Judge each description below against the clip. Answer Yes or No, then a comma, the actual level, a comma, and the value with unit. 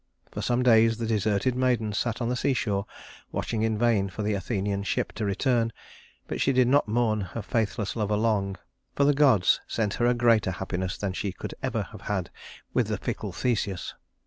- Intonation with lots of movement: No, average, 3.3 semitones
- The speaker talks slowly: No, average, 195 wpm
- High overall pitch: No, low, 110 Hz